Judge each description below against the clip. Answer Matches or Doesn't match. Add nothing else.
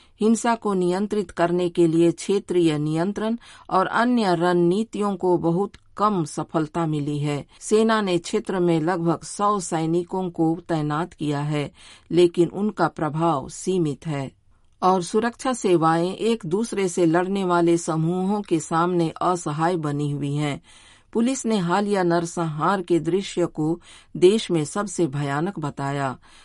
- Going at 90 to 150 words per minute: Matches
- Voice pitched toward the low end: Doesn't match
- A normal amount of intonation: Matches